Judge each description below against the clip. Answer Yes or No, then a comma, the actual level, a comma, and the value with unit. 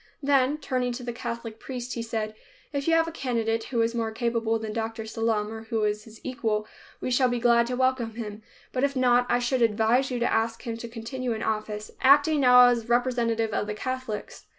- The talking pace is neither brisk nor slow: No, fast, 220 wpm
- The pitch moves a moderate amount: No, narrow, 2.3 semitones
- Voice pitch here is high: Yes, high, 235 Hz